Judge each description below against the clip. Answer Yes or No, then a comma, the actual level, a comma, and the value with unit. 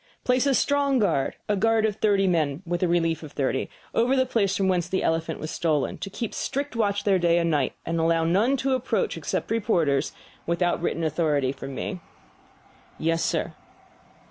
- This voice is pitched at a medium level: Yes, medium, 175 Hz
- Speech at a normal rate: Yes, average, 195 wpm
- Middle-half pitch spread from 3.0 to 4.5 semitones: No, wide, 5.4 semitones